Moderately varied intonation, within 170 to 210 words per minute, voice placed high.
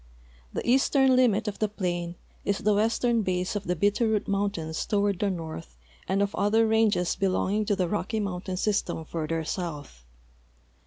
No: average, 3.4 semitones; average, 160 wpm; high, 200 Hz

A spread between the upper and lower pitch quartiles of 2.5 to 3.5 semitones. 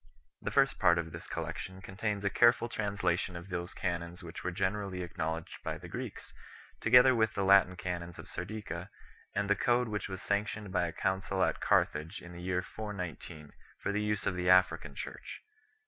Yes: average, 2.9 semitones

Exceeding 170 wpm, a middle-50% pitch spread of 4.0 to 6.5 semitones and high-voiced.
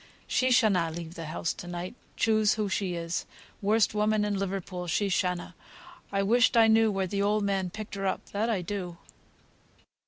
No: average, 185 wpm; average, 3.2 semitones; high, 195 Hz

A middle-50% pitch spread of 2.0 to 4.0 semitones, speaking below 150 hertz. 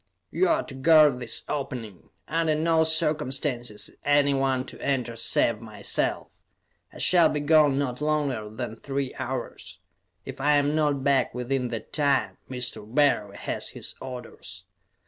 Yes: average, 3.6 semitones; low, 135 Hz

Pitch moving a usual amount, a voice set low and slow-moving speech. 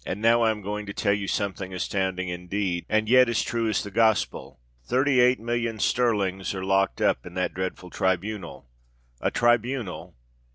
No: average, 3.7 semitones; low, 100 Hz; average, 165 wpm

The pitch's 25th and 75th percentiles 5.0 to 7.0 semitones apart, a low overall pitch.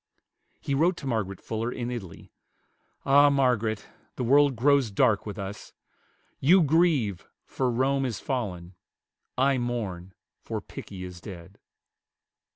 Yes: wide, 5.6 semitones; low, 120 Hz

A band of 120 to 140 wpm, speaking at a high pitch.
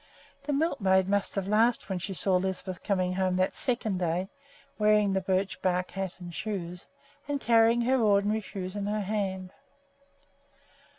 No: average, 160 wpm; high, 195 Hz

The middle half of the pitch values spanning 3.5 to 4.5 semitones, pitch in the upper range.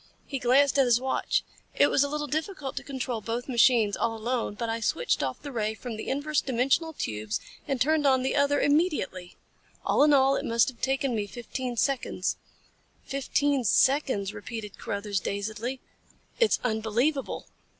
Yes: average, 4.2 semitones; very high, 255 Hz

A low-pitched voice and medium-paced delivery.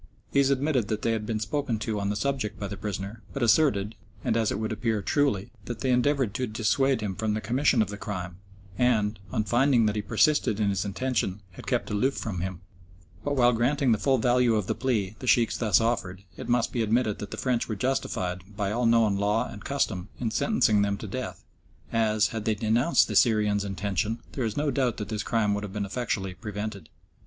No: low, 110 Hz; fast, 225 wpm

